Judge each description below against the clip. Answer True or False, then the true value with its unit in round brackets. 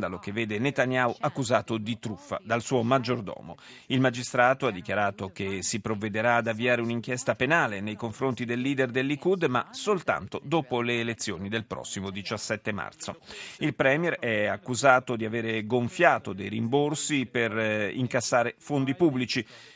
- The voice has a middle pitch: False (120 Hz)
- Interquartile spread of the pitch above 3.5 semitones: False (3.1 semitones)